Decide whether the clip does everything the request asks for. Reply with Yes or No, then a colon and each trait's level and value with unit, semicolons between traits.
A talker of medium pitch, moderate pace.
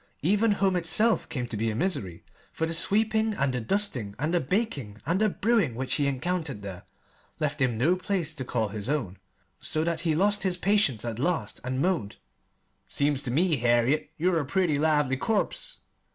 Yes: medium, 155 Hz; average, 190 wpm